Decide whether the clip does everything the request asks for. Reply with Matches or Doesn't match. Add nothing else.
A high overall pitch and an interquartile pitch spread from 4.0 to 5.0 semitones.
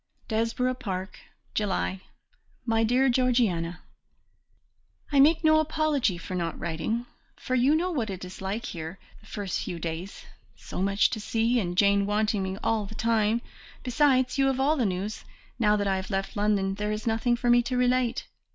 Matches